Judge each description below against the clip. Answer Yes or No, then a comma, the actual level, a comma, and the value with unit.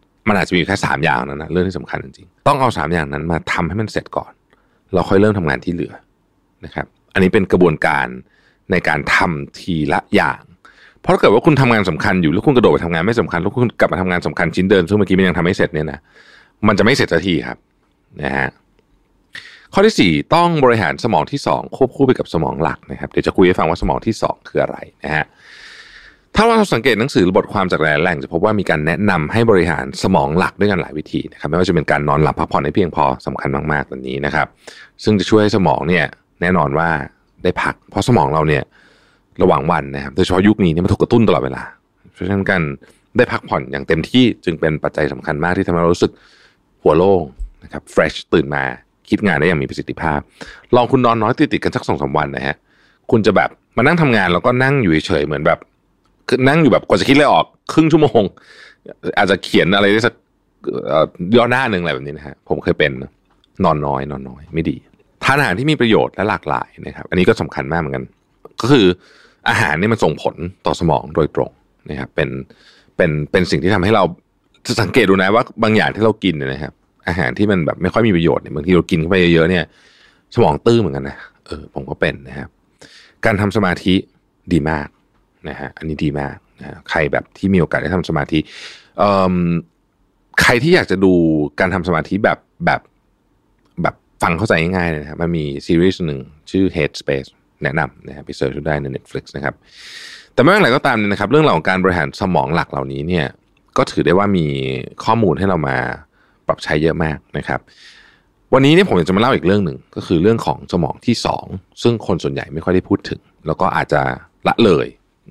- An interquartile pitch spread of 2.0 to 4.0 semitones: No, wide, 5.4 semitones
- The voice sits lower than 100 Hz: Yes, very low, 85 Hz